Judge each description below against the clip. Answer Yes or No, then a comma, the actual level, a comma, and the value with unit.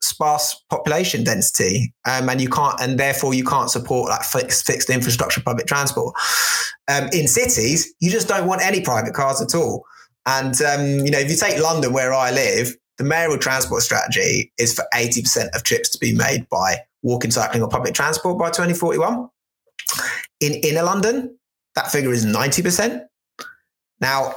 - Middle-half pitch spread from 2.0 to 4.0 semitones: No, average, 5.1 semitones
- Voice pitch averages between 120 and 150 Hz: Yes, medium, 140 Hz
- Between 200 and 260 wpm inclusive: No, average, 170 wpm